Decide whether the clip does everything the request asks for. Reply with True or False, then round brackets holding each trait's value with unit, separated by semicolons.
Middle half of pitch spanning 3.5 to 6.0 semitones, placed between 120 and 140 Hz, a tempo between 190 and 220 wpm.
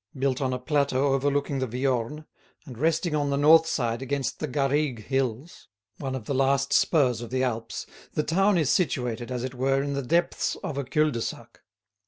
False (2.6 semitones; 135 Hz; 200 wpm)